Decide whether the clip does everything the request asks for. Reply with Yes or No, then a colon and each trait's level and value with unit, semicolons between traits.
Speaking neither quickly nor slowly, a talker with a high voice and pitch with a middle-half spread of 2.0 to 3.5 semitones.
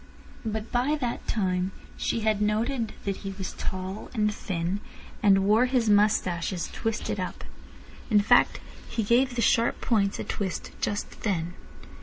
Yes: average, 150 wpm; high, 210 Hz; average, 3.0 semitones